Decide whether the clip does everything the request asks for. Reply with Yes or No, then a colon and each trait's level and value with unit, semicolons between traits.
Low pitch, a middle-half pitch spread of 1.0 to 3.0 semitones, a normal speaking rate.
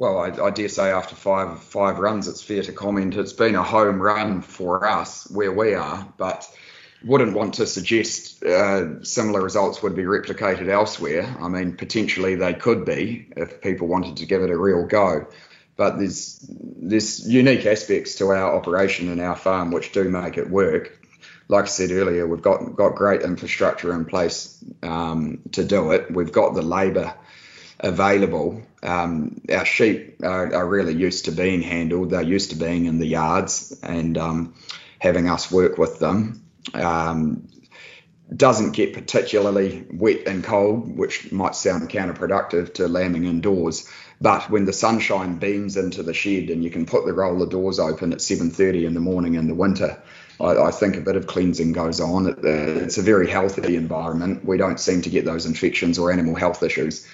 Yes: very low, 90 Hz; narrow, 2.6 semitones; average, 180 wpm